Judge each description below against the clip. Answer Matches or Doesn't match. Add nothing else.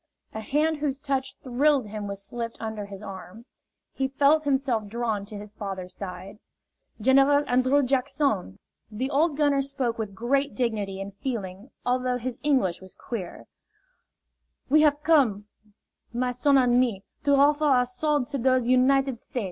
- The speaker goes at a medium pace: Matches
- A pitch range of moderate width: Matches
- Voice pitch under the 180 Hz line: Doesn't match